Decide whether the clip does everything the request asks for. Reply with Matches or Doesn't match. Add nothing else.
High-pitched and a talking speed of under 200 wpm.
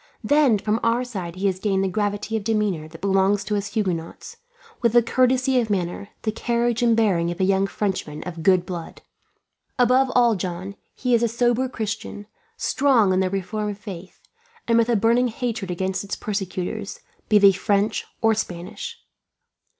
Matches